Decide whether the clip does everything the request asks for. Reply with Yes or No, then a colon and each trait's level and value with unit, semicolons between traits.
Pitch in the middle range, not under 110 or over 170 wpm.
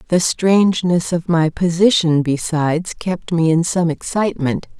Yes: medium, 170 Hz; average, 140 wpm